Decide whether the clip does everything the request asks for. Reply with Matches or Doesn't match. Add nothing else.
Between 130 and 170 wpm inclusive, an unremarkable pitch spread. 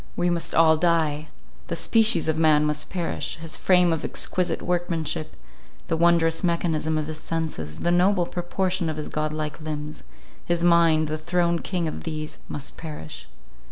Doesn't match